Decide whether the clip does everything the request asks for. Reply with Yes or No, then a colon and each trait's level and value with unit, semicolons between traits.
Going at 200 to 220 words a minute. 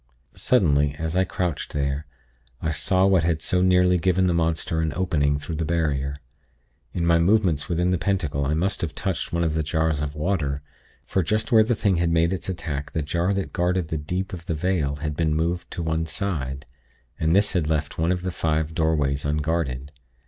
Yes: fast, 205 wpm